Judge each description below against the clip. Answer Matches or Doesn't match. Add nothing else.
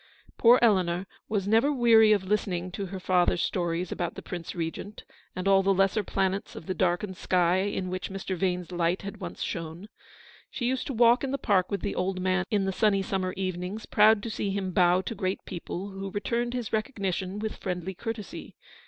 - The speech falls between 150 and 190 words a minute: Doesn't match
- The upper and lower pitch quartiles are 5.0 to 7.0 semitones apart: Doesn't match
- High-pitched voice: Matches